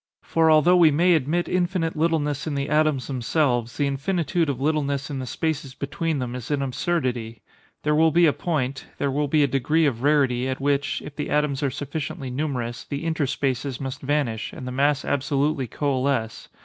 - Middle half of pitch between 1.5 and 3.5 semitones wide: Yes, average, 2.8 semitones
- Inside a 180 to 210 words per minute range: Yes, average, 185 wpm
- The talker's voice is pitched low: No, medium, 145 Hz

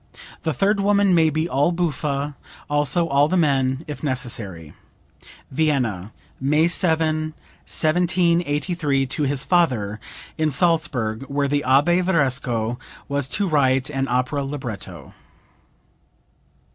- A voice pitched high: No, medium, 145 Hz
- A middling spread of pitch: Yes, average, 4.0 semitones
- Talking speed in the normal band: No, slow, 115 wpm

